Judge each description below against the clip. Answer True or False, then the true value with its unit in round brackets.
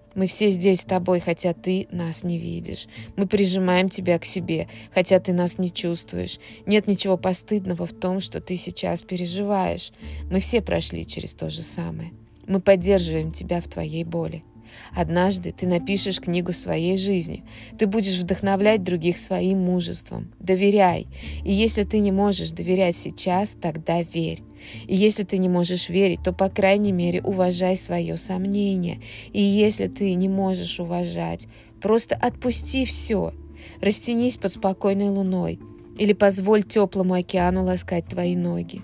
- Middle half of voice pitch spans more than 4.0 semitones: False (2.7 semitones)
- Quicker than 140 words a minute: True (150 wpm)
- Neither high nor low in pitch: True (180 Hz)